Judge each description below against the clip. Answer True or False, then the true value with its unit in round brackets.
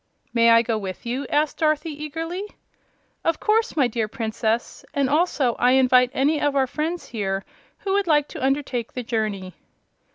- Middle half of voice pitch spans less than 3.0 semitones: False (4.8 semitones)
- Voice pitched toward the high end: True (265 Hz)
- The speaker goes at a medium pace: True (170 wpm)